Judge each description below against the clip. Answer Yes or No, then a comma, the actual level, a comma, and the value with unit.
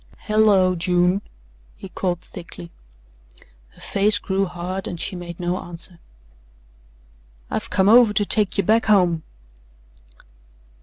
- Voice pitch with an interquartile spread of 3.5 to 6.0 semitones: No, narrow, 2.6 semitones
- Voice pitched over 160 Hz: Yes, medium, 185 Hz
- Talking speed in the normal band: No, slow, 120 wpm